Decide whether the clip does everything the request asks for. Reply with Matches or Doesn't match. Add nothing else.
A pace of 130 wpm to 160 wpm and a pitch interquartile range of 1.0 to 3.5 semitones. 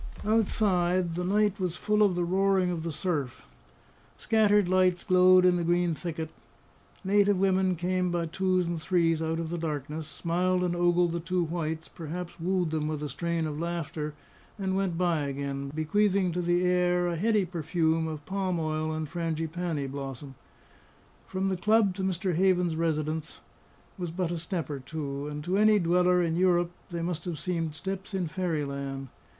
Doesn't match